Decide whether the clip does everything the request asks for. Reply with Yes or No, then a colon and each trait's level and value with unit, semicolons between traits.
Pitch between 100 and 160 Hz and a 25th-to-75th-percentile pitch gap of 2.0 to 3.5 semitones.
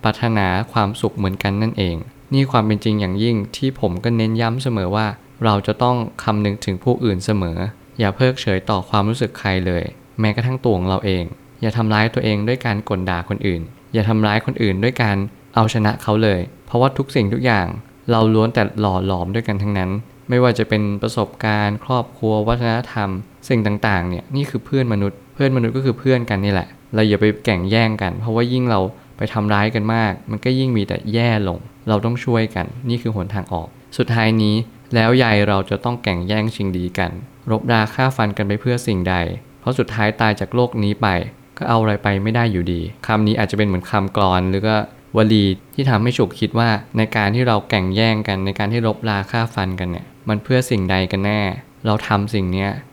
Yes: low, 110 Hz; average, 2.9 semitones